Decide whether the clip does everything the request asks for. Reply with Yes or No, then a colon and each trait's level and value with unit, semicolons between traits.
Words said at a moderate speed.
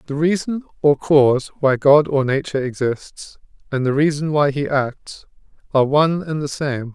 Yes: average, 175 wpm